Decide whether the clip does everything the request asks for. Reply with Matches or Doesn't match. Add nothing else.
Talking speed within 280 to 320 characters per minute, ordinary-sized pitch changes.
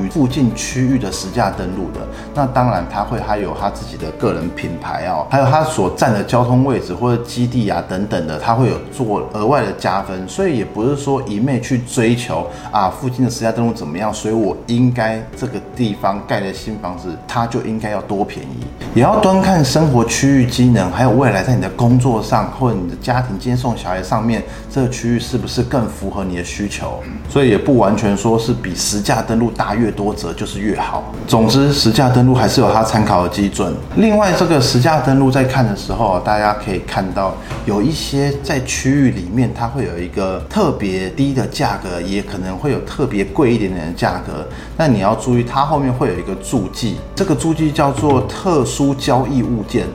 Matches